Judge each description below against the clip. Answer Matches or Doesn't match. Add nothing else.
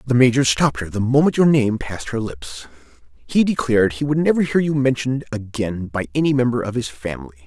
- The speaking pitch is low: Matches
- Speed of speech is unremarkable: Doesn't match